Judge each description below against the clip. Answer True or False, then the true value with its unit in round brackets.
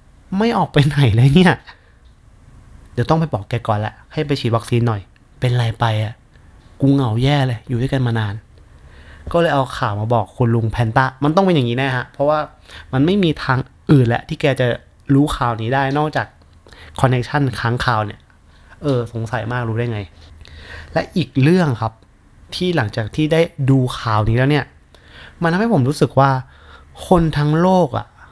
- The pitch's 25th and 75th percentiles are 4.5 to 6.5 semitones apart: True (4.9 semitones)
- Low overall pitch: True (120 Hz)